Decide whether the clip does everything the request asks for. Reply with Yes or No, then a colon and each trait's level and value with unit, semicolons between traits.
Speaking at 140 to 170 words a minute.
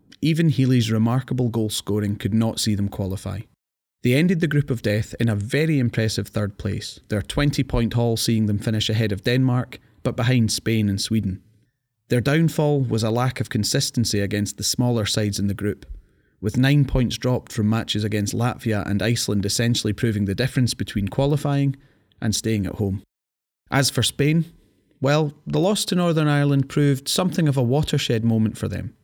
No: average, 180 wpm